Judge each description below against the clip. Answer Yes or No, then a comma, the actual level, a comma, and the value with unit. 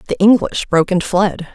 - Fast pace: No, average, 195 wpm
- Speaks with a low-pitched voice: No, high, 190 Hz